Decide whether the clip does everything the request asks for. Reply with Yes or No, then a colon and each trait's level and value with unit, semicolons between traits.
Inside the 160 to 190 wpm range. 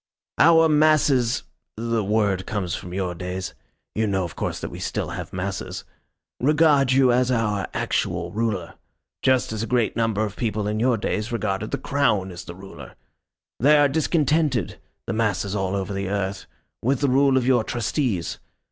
Yes: average, 175 wpm